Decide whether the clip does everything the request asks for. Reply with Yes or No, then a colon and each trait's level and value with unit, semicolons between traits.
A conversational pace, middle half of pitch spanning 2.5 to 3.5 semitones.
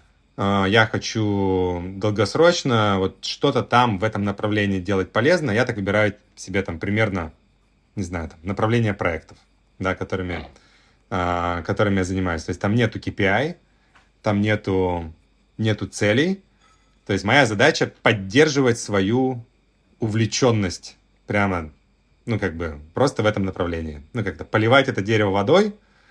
Yes: average, 135 wpm; average, 3.2 semitones